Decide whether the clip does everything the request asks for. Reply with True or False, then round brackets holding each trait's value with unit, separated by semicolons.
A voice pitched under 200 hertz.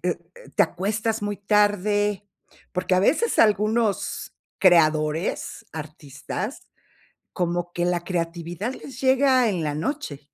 True (190 Hz)